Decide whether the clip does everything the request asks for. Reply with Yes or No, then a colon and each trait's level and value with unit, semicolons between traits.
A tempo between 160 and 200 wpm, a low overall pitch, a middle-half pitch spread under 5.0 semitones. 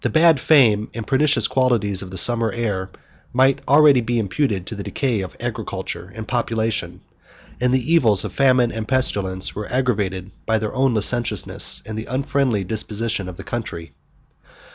Yes: average, 165 wpm; low, 115 Hz; average, 3.9 semitones